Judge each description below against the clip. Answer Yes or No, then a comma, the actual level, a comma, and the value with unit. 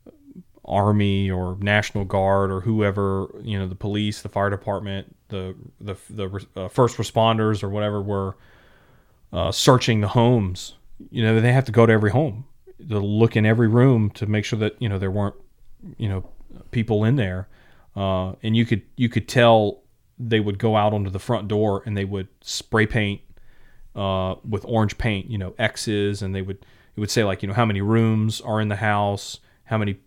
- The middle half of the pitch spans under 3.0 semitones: Yes, narrow, 2.5 semitones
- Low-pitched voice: Yes, low, 105 Hz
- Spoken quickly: No, average, 195 wpm